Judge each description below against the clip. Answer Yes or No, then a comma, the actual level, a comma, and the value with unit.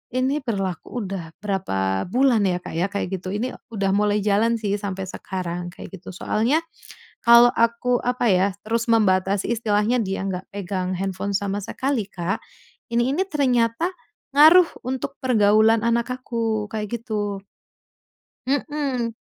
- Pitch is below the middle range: No, high, 215 Hz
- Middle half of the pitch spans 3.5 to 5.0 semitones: Yes, average, 3.9 semitones